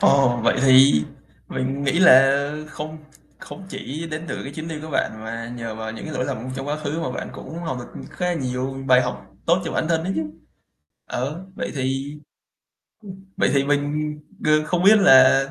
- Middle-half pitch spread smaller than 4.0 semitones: Yes, average, 3.5 semitones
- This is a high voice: No, medium, 140 Hz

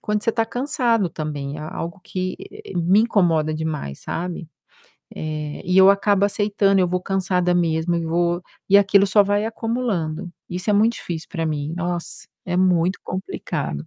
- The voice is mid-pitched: Yes, medium, 180 Hz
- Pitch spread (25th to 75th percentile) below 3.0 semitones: No, average, 3.6 semitones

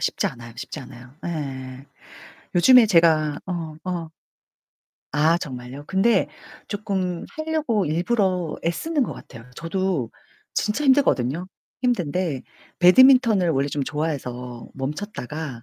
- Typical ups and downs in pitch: No, wide, 6.4 semitones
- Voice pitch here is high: No, medium, 170 Hz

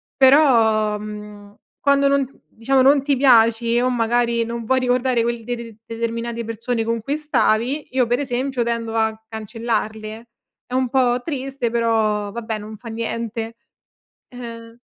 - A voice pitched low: No, high, 235 Hz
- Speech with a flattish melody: Yes, narrow, 2.2 semitones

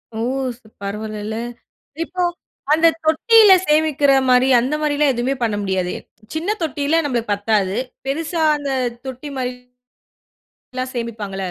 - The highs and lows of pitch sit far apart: Yes, wide, 5.8 semitones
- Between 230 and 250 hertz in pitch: No, very high, 260 Hz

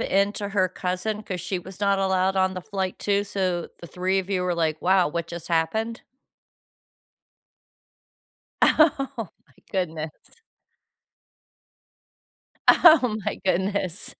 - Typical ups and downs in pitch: No, narrow, 2.2 semitones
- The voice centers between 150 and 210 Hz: Yes, high, 190 Hz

